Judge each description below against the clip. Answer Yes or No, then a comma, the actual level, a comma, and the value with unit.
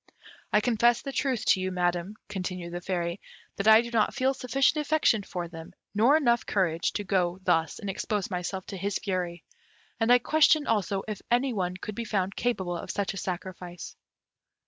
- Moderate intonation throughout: Yes, average, 4.7 semitones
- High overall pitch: Yes, high, 200 Hz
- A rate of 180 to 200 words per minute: Yes, average, 190 wpm